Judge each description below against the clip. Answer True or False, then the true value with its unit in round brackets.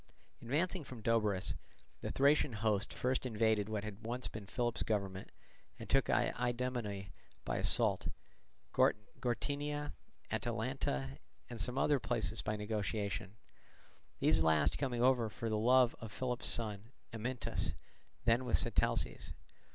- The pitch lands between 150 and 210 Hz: False (115 Hz)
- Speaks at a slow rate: True (120 wpm)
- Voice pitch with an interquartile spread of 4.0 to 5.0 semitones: False (3.4 semitones)